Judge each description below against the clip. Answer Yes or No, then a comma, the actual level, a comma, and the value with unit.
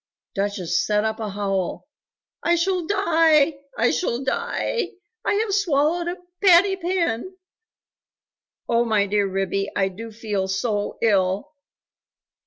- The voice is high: Yes, high, 235 Hz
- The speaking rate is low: Yes, slow, 125 wpm